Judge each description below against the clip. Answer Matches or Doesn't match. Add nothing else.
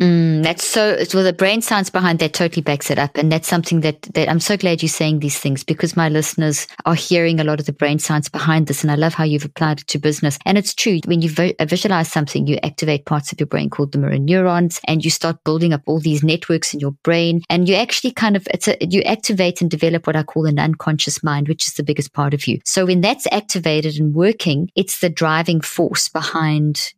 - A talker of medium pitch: Matches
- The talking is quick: Matches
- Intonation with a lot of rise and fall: Doesn't match